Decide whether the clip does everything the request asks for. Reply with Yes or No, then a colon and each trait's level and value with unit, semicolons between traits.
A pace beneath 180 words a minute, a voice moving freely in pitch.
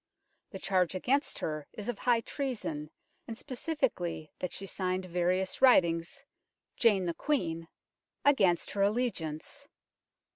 Yes: average, 140 wpm; wide, 6.4 semitones